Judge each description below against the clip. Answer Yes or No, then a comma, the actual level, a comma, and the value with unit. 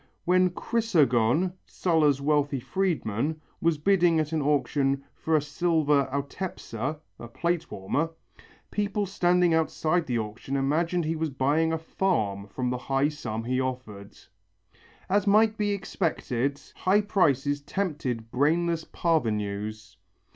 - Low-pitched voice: No, medium, 150 Hz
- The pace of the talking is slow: Yes, slow, 130 wpm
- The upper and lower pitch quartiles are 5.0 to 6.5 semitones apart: Yes, average, 5.3 semitones